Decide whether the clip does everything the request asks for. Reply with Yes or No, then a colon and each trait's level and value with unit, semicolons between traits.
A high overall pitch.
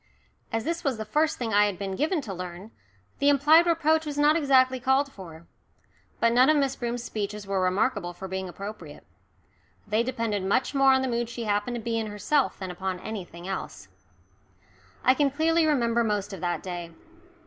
Yes: high, 230 Hz